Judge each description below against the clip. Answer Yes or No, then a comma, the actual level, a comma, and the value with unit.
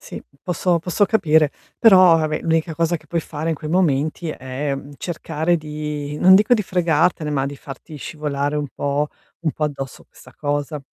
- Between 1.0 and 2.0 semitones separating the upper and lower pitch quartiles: No, average, 2.7 semitones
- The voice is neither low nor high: Yes, medium, 155 Hz